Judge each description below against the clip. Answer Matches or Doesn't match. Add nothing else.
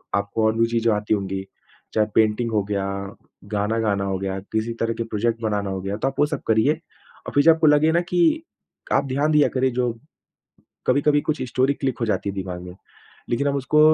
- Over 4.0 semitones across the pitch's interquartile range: Matches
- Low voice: Matches